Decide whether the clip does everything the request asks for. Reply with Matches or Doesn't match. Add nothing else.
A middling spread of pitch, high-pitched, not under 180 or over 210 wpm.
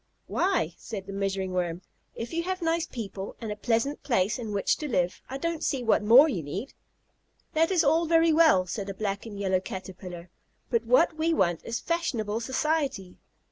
Doesn't match